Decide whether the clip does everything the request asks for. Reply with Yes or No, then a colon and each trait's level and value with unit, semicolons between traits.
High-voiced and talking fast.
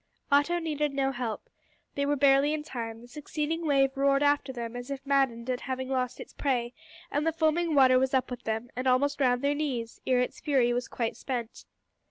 Yes: very high, 270 Hz; fast, 210 wpm